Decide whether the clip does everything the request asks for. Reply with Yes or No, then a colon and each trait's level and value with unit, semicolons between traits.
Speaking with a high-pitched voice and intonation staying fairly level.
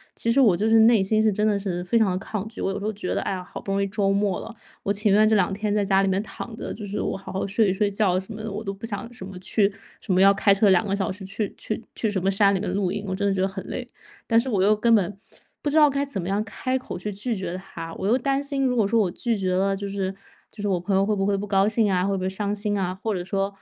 Yes: high, 200 Hz; narrow, 2.0 semitones